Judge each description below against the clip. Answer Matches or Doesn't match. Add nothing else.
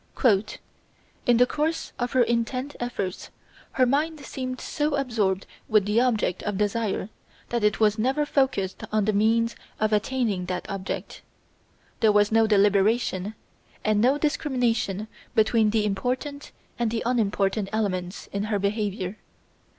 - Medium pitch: Doesn't match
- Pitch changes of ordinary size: Matches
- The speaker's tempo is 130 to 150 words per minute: Matches